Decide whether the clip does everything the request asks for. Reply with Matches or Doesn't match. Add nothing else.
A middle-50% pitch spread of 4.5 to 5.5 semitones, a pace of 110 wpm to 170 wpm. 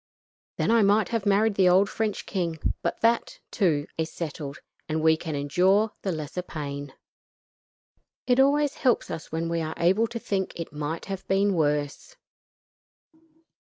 Matches